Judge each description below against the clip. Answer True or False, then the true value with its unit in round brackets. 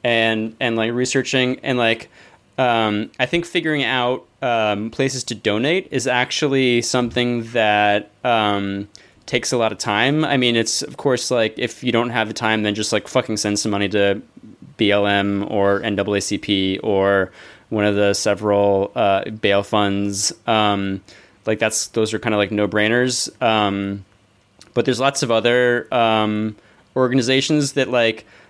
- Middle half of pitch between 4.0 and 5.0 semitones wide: False (3.4 semitones)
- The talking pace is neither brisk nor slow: True (160 wpm)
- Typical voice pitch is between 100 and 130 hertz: True (110 Hz)